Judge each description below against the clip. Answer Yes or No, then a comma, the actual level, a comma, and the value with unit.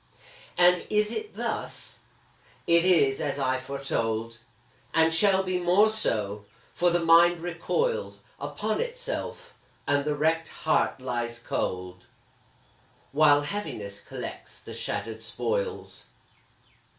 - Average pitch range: No, wide, 6.8 semitones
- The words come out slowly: Yes, slow, 115 wpm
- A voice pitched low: No, medium, 160 Hz